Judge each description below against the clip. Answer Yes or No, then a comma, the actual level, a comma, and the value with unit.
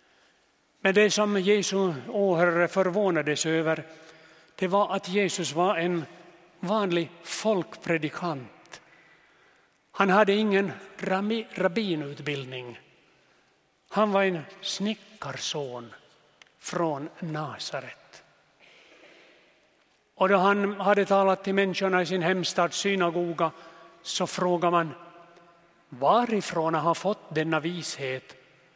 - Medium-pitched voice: Yes, medium, 180 Hz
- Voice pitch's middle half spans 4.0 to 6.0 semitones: No, average, 3.2 semitones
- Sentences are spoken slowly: Yes, slow, 90 wpm